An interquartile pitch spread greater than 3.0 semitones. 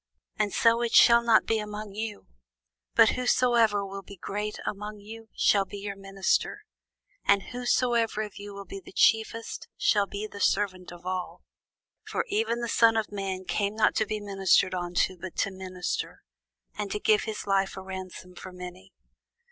No: narrow, 2.5 semitones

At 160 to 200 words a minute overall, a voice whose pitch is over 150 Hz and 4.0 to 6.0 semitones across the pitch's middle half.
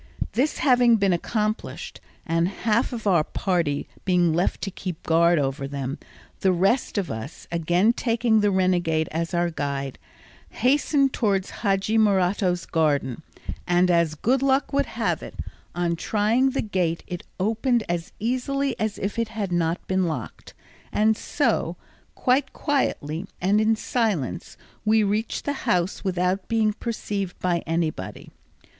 No: average, 145 wpm; high, 190 Hz; average, 4.8 semitones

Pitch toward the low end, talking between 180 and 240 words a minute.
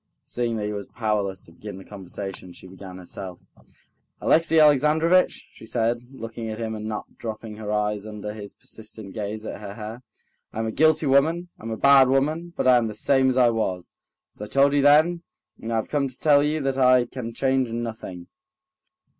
Yes: low, 115 Hz; average, 200 wpm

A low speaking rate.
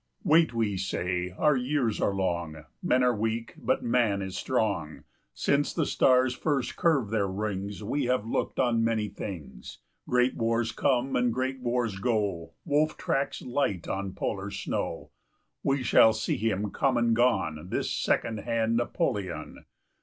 No: average, 160 wpm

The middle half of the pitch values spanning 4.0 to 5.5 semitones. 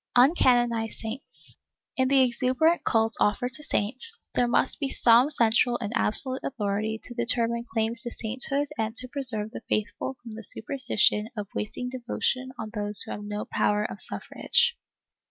No: average, 2.9 semitones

